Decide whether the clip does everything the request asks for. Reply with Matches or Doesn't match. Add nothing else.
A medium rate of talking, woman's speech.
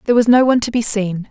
Doesn't match